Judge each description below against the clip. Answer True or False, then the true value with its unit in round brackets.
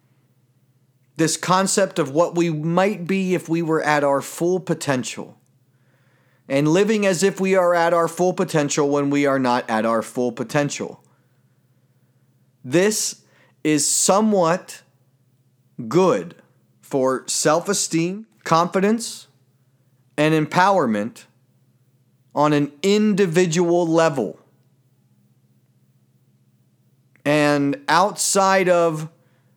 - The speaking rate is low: True (100 wpm)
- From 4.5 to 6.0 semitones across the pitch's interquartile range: True (5.3 semitones)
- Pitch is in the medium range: True (150 Hz)